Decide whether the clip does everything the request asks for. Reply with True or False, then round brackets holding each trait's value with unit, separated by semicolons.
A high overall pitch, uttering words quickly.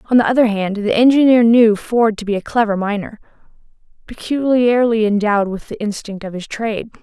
False (220 Hz; 180 wpm)